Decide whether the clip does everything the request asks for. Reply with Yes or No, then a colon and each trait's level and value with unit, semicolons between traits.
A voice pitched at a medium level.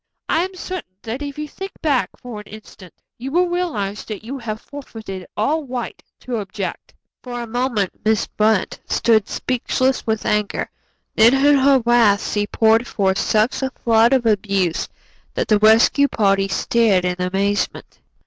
No: high, 225 Hz